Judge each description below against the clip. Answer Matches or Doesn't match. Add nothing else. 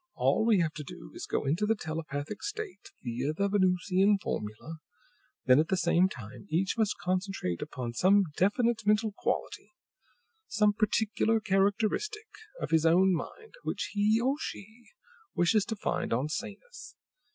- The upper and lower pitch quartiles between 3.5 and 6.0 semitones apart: Matches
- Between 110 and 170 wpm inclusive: Matches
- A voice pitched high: Matches